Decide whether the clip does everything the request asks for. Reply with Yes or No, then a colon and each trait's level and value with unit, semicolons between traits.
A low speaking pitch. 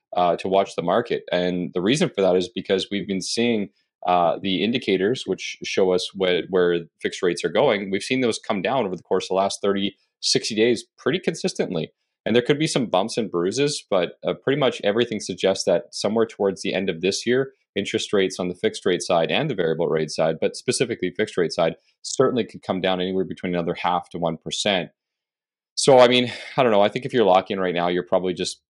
Yes: very low, 95 Hz